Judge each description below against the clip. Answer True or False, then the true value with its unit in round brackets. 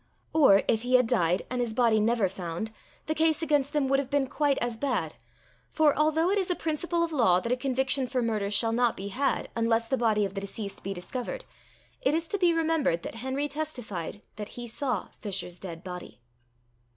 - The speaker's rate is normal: False (210 wpm)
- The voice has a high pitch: True (245 Hz)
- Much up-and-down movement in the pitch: True (5.9 semitones)